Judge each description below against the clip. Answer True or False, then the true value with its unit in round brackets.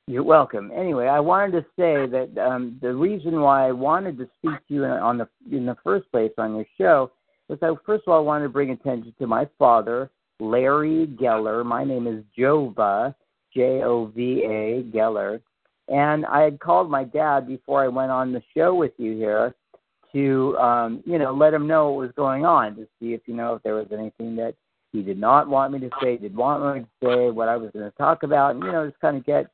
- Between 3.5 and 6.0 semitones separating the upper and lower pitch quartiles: True (3.9 semitones)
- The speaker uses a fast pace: True (225 wpm)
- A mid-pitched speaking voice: False (130 Hz)